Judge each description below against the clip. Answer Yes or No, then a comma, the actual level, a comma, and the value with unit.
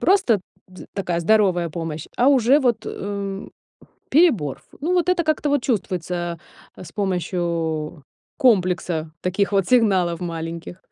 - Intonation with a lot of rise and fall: Yes, wide, 6.0 semitones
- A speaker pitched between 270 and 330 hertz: No, high, 190 Hz